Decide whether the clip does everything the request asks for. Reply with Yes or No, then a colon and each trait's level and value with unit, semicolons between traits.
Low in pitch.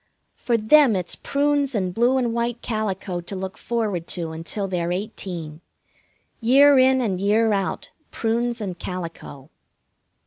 No: high, 210 Hz